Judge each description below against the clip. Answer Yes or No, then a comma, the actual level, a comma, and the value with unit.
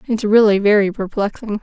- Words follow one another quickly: No, average, 145 wpm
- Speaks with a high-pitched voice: Yes, high, 210 Hz